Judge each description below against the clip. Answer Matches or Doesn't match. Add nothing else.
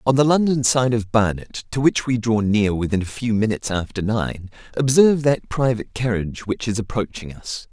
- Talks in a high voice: Doesn't match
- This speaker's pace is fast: Doesn't match